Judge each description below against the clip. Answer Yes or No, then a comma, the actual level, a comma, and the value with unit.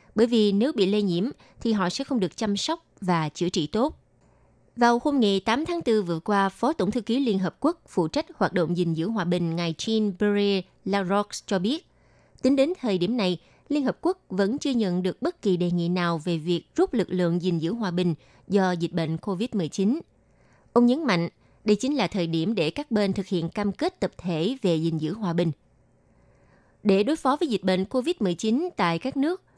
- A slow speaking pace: No, average, 215 wpm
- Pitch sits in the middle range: No, high, 200 Hz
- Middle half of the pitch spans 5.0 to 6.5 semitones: Yes, wide, 5.4 semitones